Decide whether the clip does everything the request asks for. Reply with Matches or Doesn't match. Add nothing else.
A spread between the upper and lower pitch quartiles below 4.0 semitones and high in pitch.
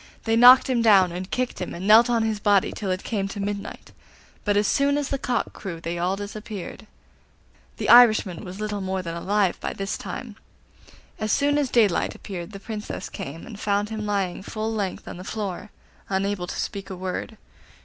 Matches